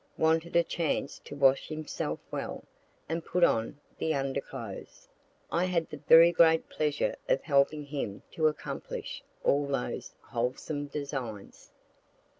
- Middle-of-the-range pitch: Yes, medium, 150 Hz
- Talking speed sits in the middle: No, slow, 130 wpm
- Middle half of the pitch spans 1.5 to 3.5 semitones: Yes, average, 2.8 semitones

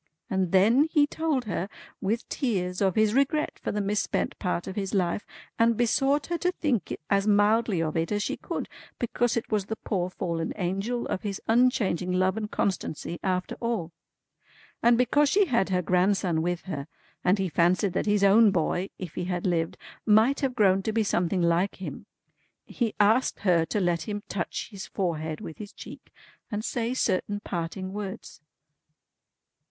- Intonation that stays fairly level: No, average, 4.0 semitones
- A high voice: Yes, high, 200 Hz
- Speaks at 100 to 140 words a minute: No, average, 180 wpm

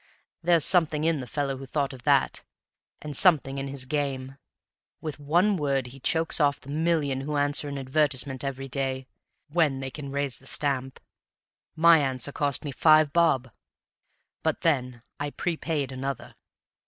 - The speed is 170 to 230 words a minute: No, average, 160 wpm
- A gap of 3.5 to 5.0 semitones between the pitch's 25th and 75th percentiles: No, narrow, 2.5 semitones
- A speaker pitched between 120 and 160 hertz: Yes, medium, 140 Hz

